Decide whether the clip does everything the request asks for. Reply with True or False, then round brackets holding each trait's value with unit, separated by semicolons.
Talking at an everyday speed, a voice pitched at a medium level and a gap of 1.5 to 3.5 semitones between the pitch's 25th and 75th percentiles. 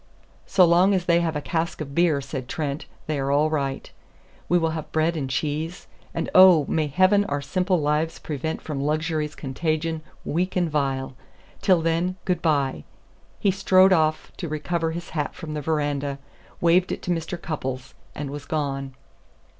True (175 wpm; 155 Hz; 3.0 semitones)